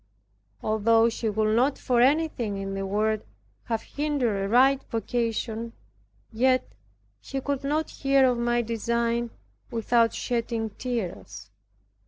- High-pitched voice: Yes, high, 235 Hz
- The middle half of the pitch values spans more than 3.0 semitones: No, average, 2.7 semitones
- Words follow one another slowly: Yes, slow, 125 wpm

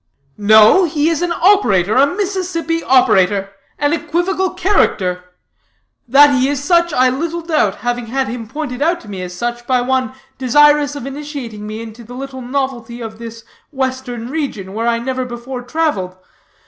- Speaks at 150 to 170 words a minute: Yes, average, 165 wpm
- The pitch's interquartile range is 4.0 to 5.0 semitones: Yes, average, 4.6 semitones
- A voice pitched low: No, very high, 260 Hz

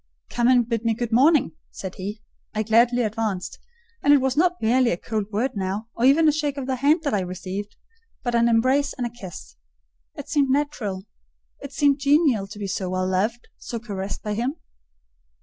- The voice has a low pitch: No, high, 235 Hz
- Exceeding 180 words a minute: Yes, average, 200 wpm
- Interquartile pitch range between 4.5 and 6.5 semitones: Yes, average, 4.9 semitones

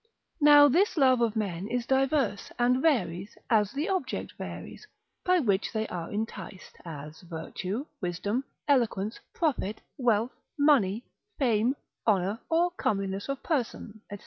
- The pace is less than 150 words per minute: Yes, slow, 135 wpm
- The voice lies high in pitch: Yes, high, 225 Hz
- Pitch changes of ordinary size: No, wide, 5.8 semitones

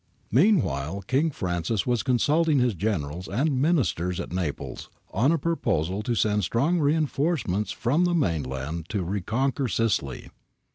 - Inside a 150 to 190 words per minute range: No, average, 140 wpm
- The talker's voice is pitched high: No, low, 110 Hz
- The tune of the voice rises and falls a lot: Yes, wide, 8.3 semitones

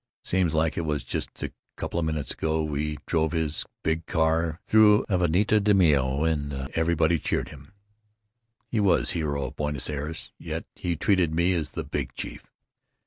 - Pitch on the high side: No, very low, 80 Hz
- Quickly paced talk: No, average, 165 wpm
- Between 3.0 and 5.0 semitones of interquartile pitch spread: No, narrow, 2.4 semitones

